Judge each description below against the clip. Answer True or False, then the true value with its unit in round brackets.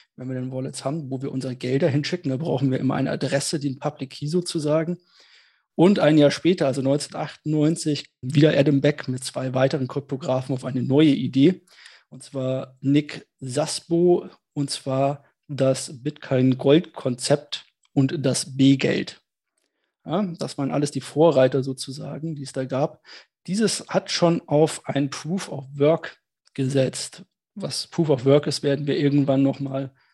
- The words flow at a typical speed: True (145 wpm)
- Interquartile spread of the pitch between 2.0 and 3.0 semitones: True (2.5 semitones)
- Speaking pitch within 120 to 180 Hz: True (140 Hz)